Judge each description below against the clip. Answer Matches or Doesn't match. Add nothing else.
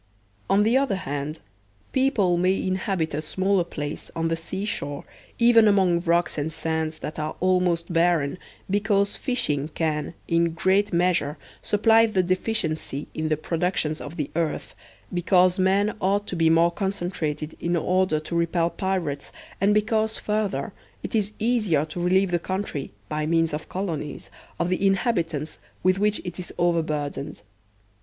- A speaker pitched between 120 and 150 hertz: Doesn't match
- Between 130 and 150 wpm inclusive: Doesn't match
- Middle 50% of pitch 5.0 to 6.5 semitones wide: Doesn't match